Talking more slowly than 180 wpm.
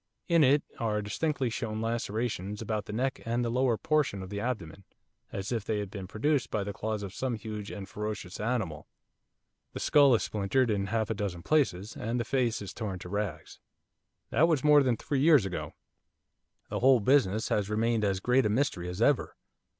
No: average, 195 wpm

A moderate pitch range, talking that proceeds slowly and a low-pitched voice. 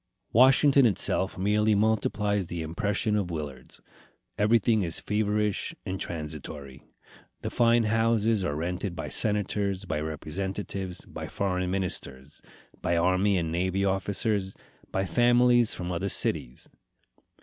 Yes: average, 3.5 semitones; slow, 120 wpm; very low, 95 Hz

